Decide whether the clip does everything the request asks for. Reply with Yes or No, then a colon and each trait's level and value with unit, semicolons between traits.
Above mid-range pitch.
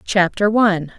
Yes: high, 195 Hz